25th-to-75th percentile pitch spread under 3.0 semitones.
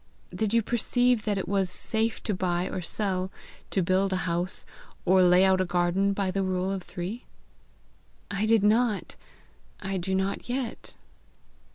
Yes: narrow, 2.5 semitones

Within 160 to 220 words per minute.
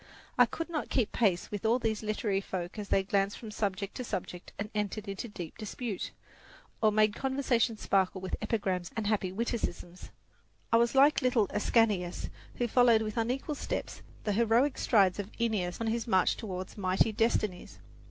Yes: average, 170 wpm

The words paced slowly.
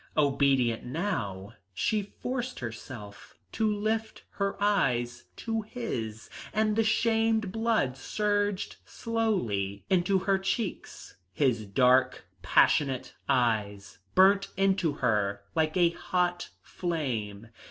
Yes: slow, 105 wpm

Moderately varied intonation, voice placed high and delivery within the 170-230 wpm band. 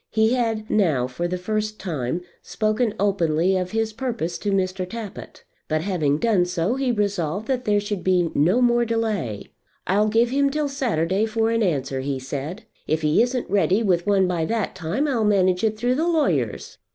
Yes: average, 4.6 semitones; high, 205 Hz; average, 190 wpm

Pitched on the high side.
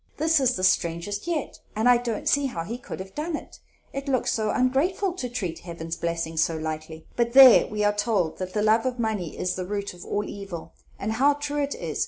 Yes: high, 215 Hz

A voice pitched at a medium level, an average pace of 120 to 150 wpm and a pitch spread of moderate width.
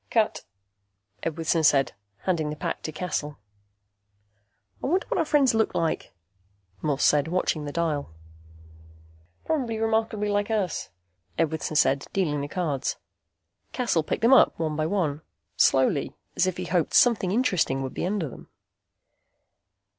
No: medium, 170 Hz; average, 140 wpm; wide, 6.3 semitones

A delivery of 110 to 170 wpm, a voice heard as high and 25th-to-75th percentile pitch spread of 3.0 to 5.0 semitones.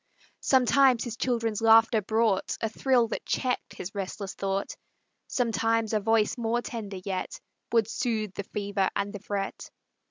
No: average, 150 wpm; high, 225 Hz; narrow, 2.6 semitones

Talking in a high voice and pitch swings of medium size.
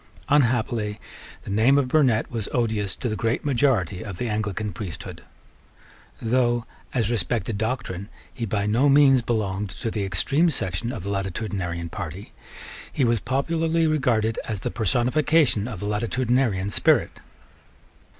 No: low, 115 Hz; average, 4.0 semitones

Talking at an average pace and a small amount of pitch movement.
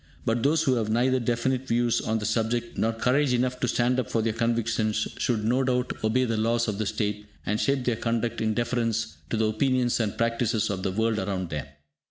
No: fast, 220 wpm; narrow, 2.2 semitones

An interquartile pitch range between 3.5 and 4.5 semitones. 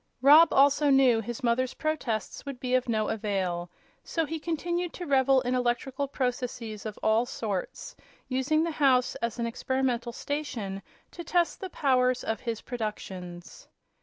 Yes: average, 4.0 semitones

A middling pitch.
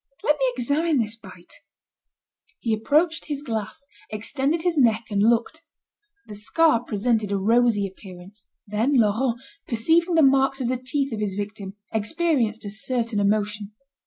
No: high, 230 Hz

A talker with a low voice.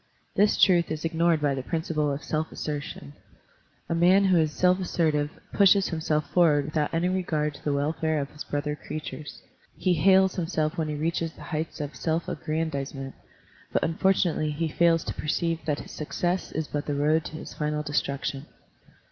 No: medium, 155 Hz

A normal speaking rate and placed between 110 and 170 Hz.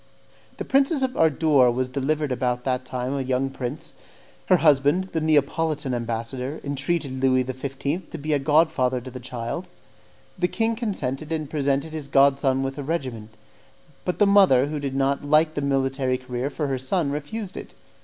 Yes: average, 180 wpm; medium, 140 Hz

